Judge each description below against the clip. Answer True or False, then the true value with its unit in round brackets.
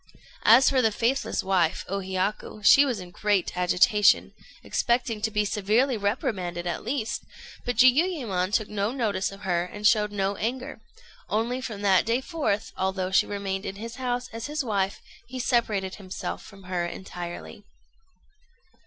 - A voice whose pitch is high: True (210 Hz)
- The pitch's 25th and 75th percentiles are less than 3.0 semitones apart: False (4.1 semitones)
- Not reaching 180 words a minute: True (160 wpm)